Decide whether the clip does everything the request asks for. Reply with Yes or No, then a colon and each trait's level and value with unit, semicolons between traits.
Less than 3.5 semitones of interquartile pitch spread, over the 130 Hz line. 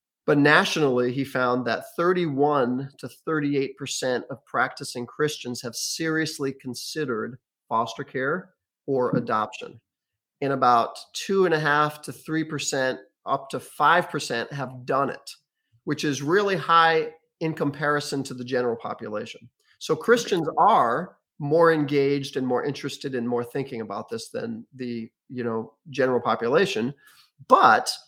No: average, 3.8 semitones; medium, 140 Hz